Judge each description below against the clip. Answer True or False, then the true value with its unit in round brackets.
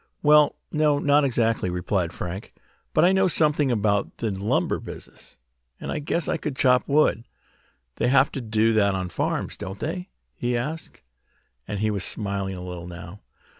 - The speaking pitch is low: True (115 Hz)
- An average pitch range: False (7.0 semitones)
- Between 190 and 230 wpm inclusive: False (170 wpm)